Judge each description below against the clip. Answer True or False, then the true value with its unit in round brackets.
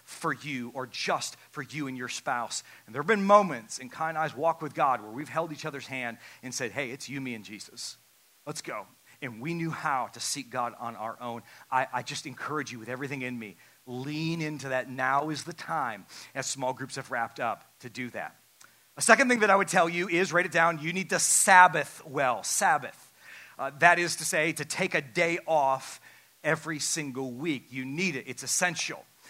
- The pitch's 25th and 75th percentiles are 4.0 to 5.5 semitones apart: True (4.4 semitones)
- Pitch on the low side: False (145 Hz)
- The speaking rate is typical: False (220 wpm)